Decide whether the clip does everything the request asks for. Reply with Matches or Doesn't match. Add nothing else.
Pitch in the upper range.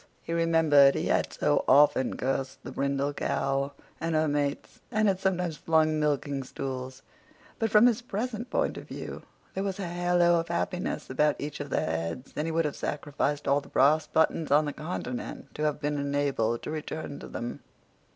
Doesn't match